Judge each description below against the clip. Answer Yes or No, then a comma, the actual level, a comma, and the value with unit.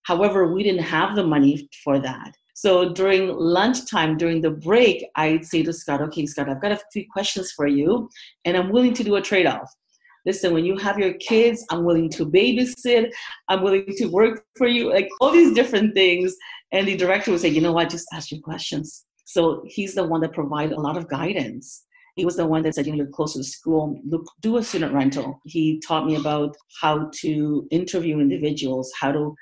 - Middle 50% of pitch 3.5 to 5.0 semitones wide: Yes, average, 4.2 semitones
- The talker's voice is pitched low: No, medium, 170 Hz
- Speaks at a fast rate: Yes, fast, 210 wpm